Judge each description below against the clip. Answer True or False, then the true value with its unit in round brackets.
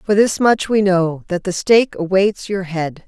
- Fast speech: True (215 wpm)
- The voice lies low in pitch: False (190 Hz)